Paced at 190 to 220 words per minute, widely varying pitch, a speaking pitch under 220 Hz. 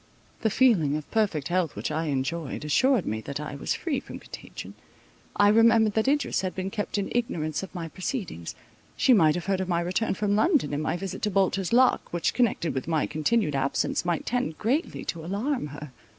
Yes: fast, 205 wpm; wide, 6.3 semitones; medium, 185 Hz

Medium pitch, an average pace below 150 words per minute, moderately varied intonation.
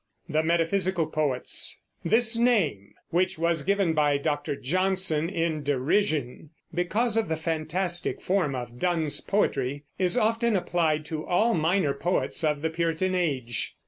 Yes: medium, 165 Hz; average, 140 wpm; average, 3.8 semitones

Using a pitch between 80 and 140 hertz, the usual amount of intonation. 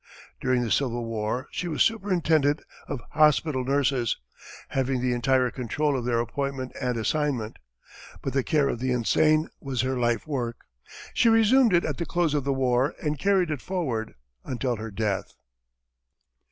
Yes: low, 135 Hz; average, 4.0 semitones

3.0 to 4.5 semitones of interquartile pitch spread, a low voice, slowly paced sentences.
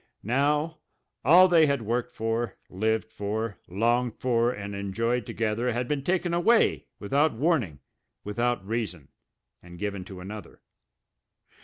No: average, 5.2 semitones; low, 115 Hz; slow, 130 wpm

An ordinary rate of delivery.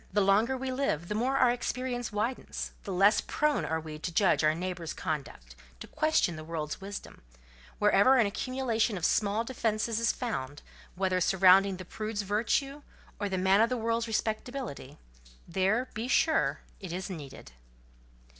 Yes: average, 165 wpm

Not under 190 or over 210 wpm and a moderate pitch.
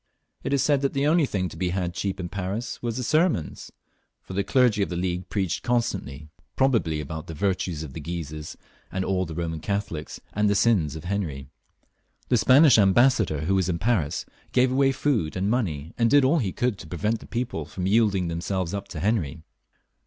No: average, 200 wpm; very low, 95 Hz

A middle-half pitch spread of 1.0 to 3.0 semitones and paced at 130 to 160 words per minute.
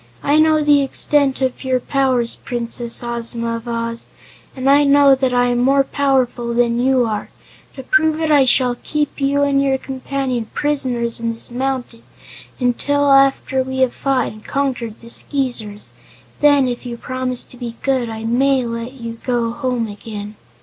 No: narrow, 2.6 semitones; average, 170 wpm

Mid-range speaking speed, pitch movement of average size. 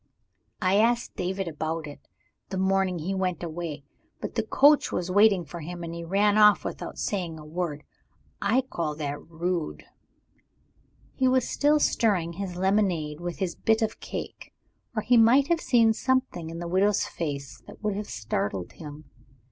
Yes: average, 170 wpm; average, 4.5 semitones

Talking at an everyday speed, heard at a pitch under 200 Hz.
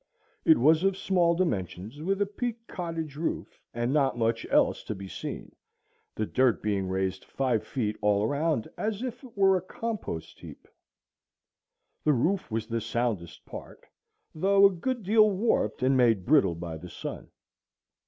Yes: average, 165 wpm; medium, 140 Hz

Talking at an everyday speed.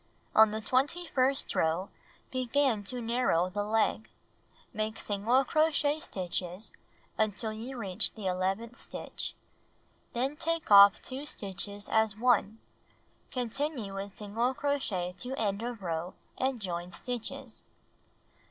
No: slow, 125 wpm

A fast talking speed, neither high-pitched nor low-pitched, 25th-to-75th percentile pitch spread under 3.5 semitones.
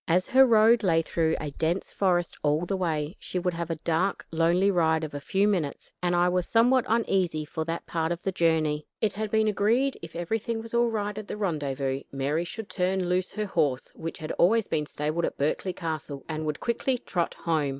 No: fast, 220 wpm; medium, 175 Hz; average, 4.3 semitones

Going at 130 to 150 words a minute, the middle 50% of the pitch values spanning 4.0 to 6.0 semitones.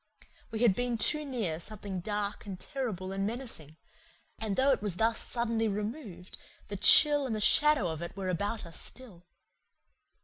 No: average, 165 wpm; average, 4.5 semitones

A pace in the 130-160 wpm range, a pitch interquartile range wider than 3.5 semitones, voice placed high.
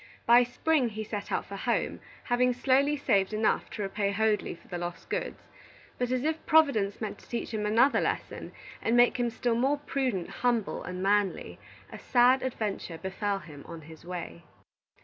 No: average, 180 wpm; average, 4.2 semitones; high, 220 Hz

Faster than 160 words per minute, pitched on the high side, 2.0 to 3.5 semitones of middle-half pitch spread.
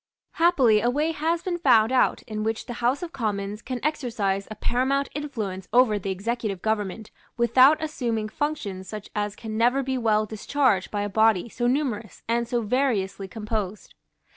No: average, 170 wpm; high, 230 Hz; average, 3.9 semitones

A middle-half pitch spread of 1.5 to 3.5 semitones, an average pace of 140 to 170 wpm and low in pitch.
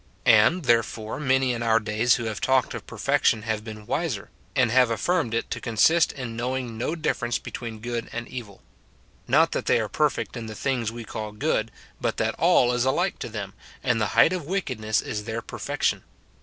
No: average, 3.1 semitones; average, 195 wpm; low, 120 Hz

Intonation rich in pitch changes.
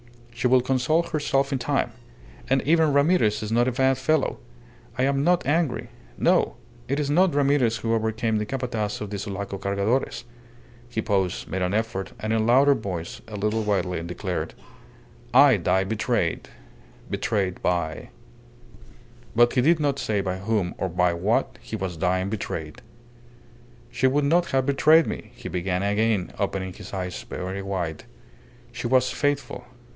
Yes: wide, 5.8 semitones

